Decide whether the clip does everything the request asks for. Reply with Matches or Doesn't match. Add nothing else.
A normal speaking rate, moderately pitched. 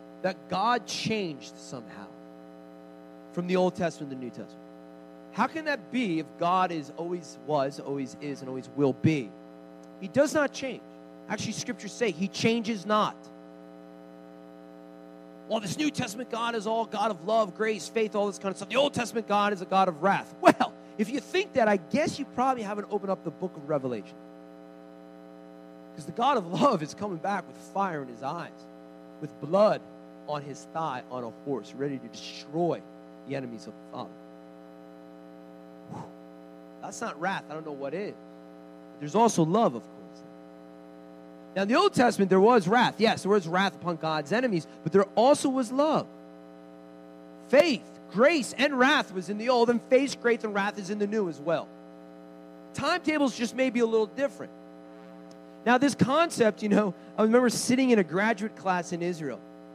Matches